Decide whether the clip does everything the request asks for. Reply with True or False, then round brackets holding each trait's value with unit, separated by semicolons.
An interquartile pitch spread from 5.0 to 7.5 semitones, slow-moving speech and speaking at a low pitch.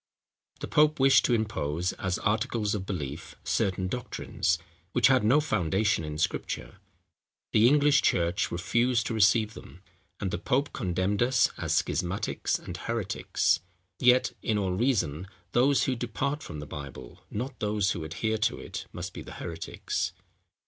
False (5.3 semitones; 155 wpm; 105 Hz)